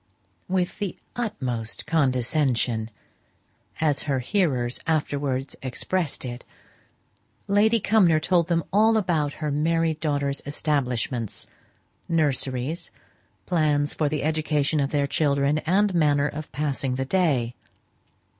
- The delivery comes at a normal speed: No, slow, 110 wpm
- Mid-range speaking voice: Yes, medium, 150 Hz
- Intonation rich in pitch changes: No, average, 3.7 semitones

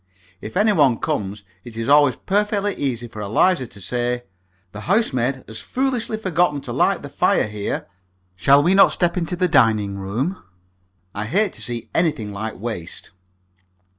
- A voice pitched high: No, low, 130 Hz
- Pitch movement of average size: No, wide, 8.7 semitones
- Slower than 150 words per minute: No, average, 165 wpm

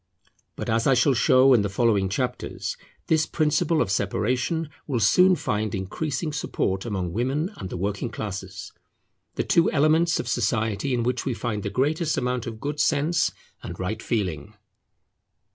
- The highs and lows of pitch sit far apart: Yes, wide, 6.1 semitones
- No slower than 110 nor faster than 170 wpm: Yes, average, 160 wpm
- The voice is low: Yes, low, 120 Hz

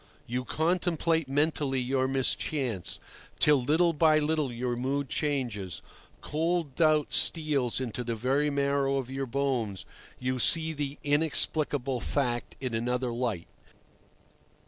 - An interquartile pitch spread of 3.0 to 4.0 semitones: Yes, average, 3.4 semitones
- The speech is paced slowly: Yes, slow, 125 wpm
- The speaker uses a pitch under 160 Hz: Yes, low, 135 Hz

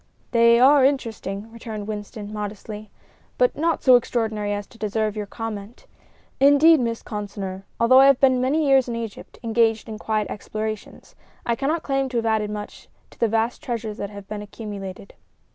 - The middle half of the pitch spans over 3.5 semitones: No, average, 3.2 semitones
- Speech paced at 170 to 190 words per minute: Yes, average, 175 wpm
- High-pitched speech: Yes, high, 225 Hz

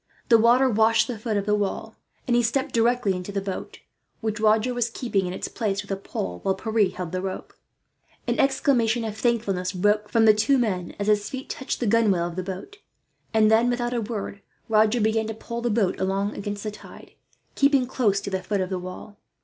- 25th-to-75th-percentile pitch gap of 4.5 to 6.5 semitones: No, average, 3.2 semitones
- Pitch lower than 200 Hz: No, high, 215 Hz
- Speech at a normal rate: No, fast, 220 wpm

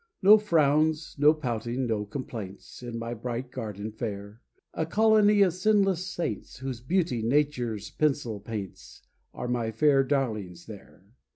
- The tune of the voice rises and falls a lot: Yes, wide, 5.8 semitones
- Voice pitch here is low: Yes, low, 125 Hz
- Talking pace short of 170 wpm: Yes, slow, 135 wpm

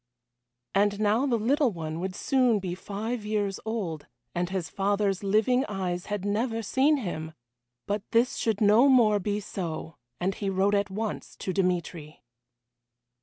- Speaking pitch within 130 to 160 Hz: No, high, 205 Hz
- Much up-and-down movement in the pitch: No, average, 3.2 semitones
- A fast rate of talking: No, average, 155 wpm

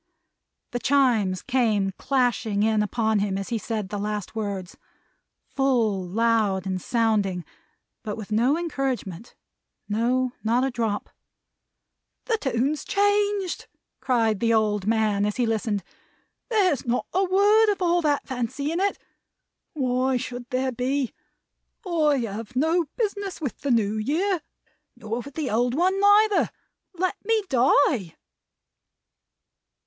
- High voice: Yes, high, 245 Hz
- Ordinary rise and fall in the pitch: No, wide, 6.1 semitones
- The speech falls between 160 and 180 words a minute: No, slow, 135 wpm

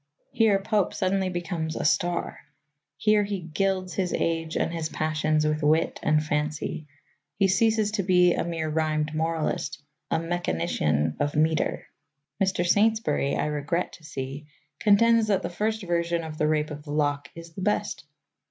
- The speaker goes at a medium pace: Yes, average, 160 wpm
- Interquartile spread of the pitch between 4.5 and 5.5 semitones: No, average, 3.9 semitones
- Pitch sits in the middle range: Yes, medium, 165 Hz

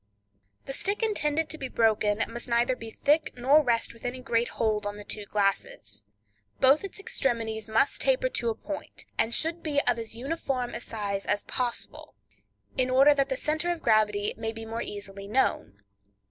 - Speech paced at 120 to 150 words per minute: No, average, 185 wpm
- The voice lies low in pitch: No, high, 235 Hz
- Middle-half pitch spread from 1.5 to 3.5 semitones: No, average, 4.8 semitones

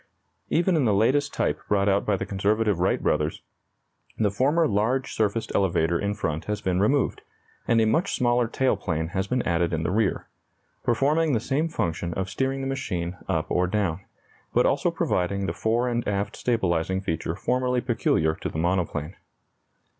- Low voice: Yes, low, 105 Hz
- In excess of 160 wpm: Yes, average, 175 wpm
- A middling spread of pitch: No, wide, 5.7 semitones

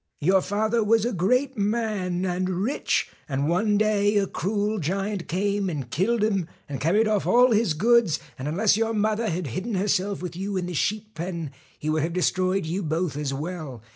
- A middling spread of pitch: Yes, average, 4.0 semitones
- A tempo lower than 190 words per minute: No, average, 195 wpm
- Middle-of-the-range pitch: No, high, 195 Hz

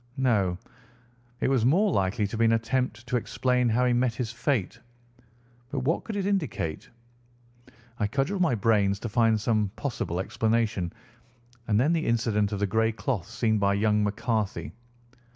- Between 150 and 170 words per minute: Yes, average, 165 wpm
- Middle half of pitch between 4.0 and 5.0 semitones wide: No, average, 3.4 semitones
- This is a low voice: Yes, low, 115 Hz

